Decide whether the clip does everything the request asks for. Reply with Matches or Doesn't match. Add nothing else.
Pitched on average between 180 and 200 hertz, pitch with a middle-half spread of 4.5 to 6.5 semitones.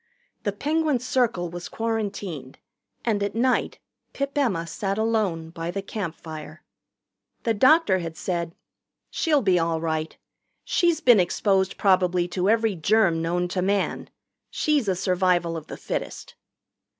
Matches